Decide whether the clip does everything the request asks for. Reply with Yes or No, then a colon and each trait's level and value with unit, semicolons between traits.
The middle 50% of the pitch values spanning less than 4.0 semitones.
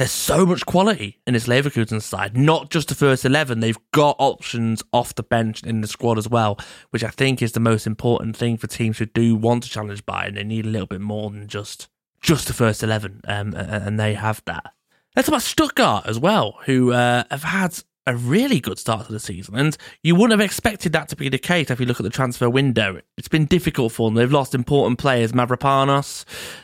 No: average, 4.6 semitones